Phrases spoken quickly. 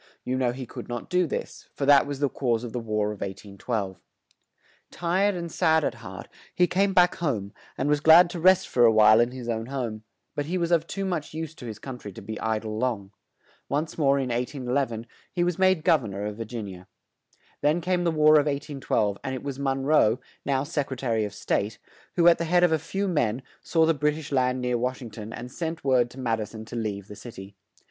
Yes: fast, 250 wpm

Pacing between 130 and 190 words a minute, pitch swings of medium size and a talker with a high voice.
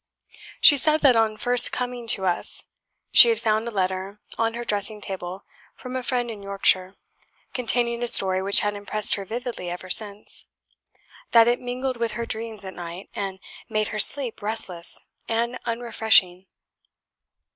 Yes: average, 160 wpm; average, 3.6 semitones; high, 220 Hz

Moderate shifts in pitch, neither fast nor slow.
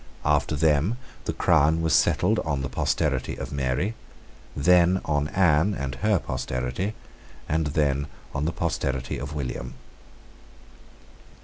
No: average, 3.4 semitones; slow, 125 wpm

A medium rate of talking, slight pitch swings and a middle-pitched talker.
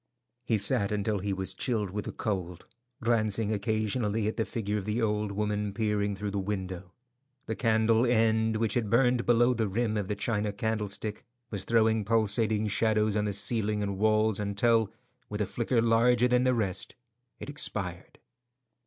No: average, 170 wpm; narrow, 1.9 semitones; low, 110 Hz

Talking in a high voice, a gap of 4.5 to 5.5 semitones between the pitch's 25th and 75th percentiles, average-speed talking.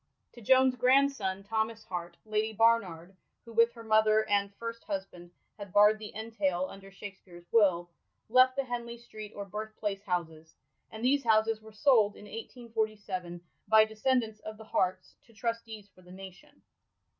No: high, 215 Hz; average, 2.8 semitones; average, 165 wpm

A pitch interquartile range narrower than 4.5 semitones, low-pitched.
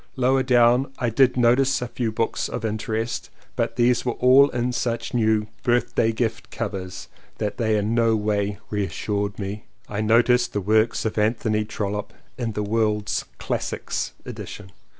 Yes: narrow, 2.5 semitones; low, 115 Hz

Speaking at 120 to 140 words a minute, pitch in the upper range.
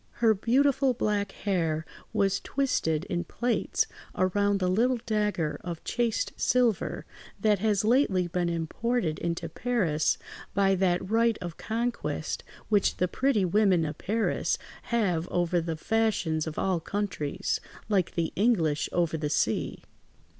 Yes: slow, 135 wpm; high, 195 Hz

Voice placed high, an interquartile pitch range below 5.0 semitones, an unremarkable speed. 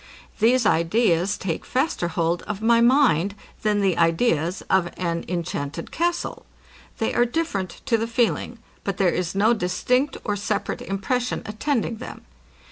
No: high, 205 Hz; wide, 5.4 semitones; average, 145 wpm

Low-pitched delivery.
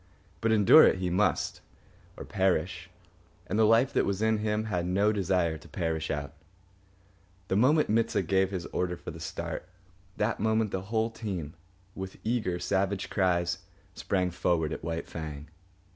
Yes: very low, 95 Hz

